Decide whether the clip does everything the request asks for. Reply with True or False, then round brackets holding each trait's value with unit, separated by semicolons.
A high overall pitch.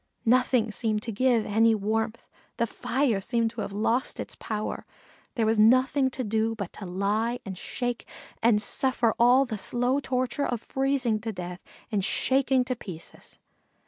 True (230 Hz)